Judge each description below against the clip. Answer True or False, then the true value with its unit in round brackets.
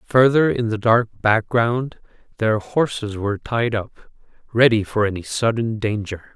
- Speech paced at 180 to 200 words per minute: False (140 wpm)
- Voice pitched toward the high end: False (110 Hz)